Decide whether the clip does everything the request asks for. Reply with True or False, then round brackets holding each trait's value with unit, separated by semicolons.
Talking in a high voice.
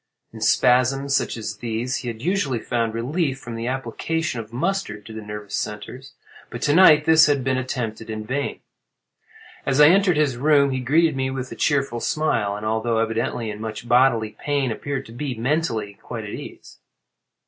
False (125 Hz)